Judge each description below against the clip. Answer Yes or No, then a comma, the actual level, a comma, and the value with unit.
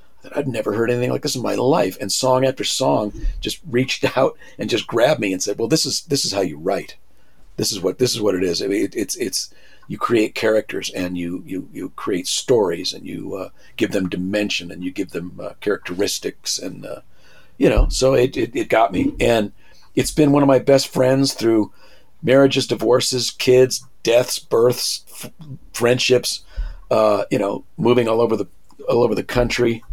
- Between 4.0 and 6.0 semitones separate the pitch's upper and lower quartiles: Yes, average, 4.4 semitones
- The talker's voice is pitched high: No, low, 125 Hz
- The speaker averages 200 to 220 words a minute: Yes, fast, 205 wpm